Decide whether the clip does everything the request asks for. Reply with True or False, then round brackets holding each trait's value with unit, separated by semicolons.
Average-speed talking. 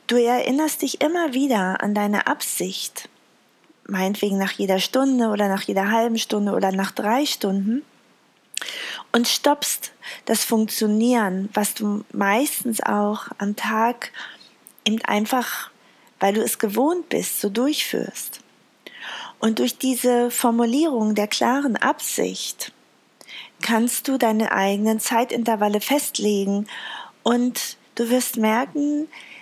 False (115 wpm)